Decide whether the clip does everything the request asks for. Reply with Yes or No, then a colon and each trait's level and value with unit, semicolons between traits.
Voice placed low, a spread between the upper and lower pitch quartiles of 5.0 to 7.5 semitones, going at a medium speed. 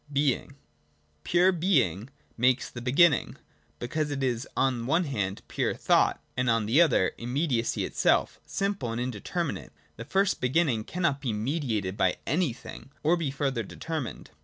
Yes: low, 130 Hz; wide, 5.4 semitones; average, 160 wpm